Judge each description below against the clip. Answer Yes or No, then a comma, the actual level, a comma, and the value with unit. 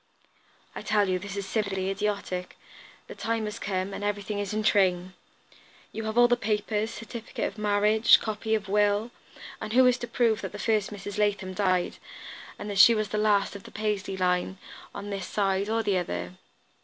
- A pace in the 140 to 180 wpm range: No, average, 190 wpm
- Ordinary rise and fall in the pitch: No, narrow, 1.9 semitones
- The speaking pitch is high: Yes, high, 205 Hz